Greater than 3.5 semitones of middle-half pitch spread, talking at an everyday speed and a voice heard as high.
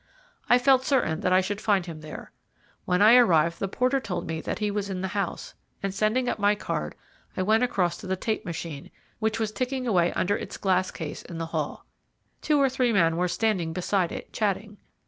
No: average, 4.1 semitones; fast, 215 wpm; high, 200 Hz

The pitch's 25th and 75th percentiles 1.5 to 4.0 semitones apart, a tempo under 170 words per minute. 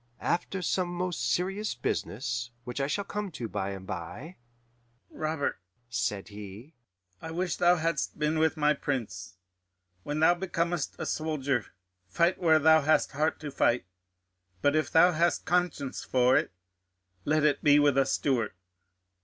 No: wide, 5.4 semitones; average, 155 wpm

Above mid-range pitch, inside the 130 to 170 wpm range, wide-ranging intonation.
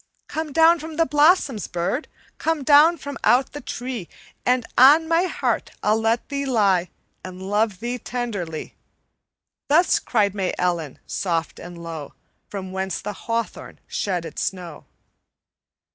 Yes: high, 225 Hz; average, 145 wpm; wide, 7.5 semitones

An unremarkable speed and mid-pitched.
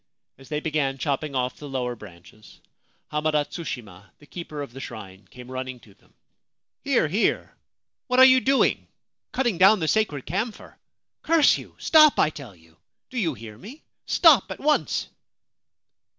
Yes: average, 165 wpm; medium, 150 Hz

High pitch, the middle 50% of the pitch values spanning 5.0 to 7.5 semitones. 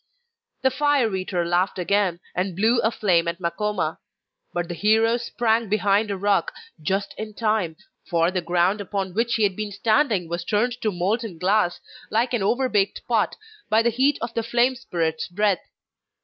No: high, 205 Hz; average, 4.0 semitones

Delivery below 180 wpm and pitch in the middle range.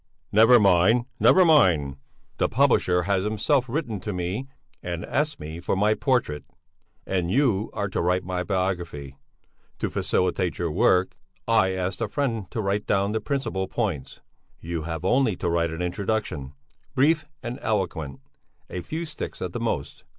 No: average, 160 wpm; very low, 95 Hz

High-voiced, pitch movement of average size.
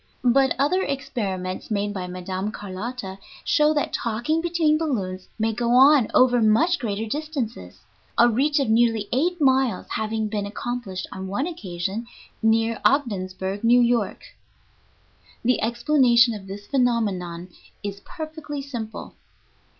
Yes: high, 230 Hz; average, 5.0 semitones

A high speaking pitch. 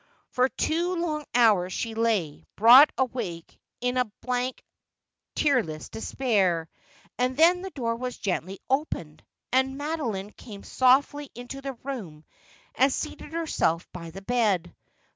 Yes: high, 245 Hz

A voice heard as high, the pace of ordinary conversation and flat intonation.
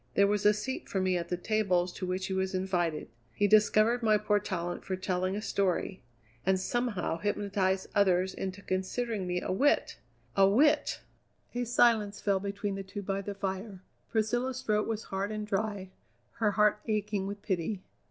Yes: high, 200 Hz; average, 180 wpm; narrow, 2.1 semitones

